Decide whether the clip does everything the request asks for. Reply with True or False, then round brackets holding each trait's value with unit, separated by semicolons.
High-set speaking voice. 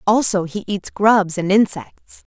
True (195 Hz)